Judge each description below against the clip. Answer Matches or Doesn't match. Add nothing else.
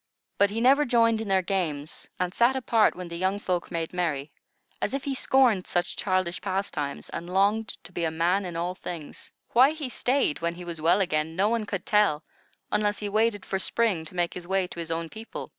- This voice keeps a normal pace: Doesn't match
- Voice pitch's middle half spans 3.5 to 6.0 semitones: Matches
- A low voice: Doesn't match